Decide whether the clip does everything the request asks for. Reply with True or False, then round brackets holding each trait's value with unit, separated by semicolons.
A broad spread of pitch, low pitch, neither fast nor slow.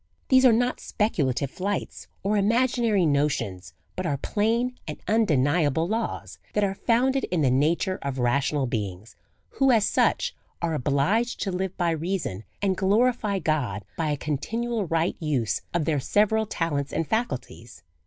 False (7.5 semitones; 175 Hz; 155 wpm)